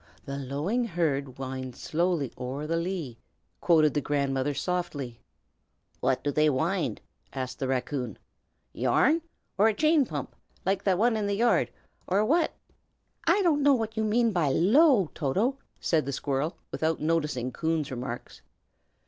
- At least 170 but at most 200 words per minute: No, average, 150 wpm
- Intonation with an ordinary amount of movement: No, wide, 7.5 semitones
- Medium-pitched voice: Yes, medium, 160 Hz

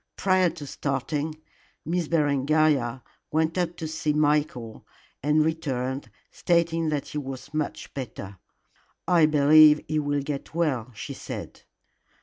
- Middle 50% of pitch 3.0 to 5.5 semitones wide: No, narrow, 2.5 semitones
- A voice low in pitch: No, medium, 150 Hz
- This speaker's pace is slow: Yes, slow, 130 wpm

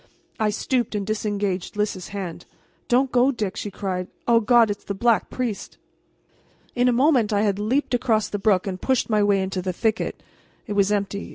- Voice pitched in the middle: No, high, 210 Hz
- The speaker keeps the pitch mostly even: No, average, 3.1 semitones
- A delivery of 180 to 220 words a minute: Yes, average, 190 wpm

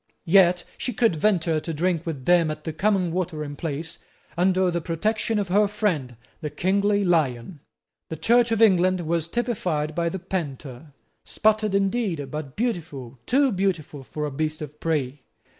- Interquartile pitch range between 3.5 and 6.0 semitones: Yes, average, 4.6 semitones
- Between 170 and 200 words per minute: No, average, 160 wpm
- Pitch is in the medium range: Yes, medium, 170 Hz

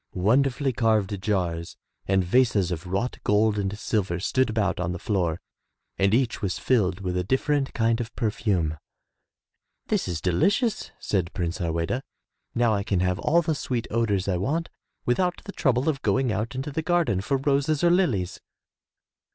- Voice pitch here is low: Yes, low, 110 Hz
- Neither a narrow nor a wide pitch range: No, wide, 6.3 semitones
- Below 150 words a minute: No, average, 170 wpm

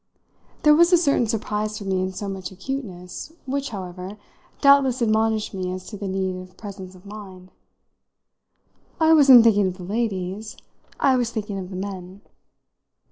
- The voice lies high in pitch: Yes, high, 205 Hz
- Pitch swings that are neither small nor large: Yes, average, 4.1 semitones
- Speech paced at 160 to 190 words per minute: Yes, average, 165 wpm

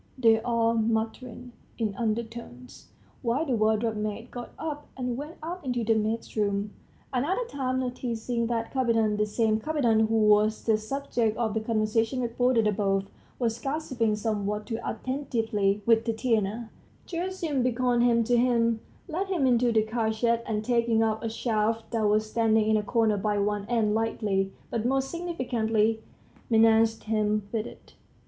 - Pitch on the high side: Yes, high, 225 Hz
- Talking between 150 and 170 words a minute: Yes, average, 155 wpm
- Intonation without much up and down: Yes, narrow, 2.3 semitones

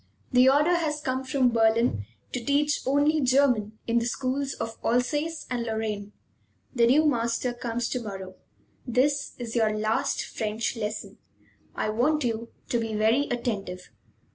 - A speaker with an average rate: Yes, average, 150 wpm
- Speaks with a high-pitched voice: Yes, high, 240 Hz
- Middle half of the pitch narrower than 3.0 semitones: No, average, 3.6 semitones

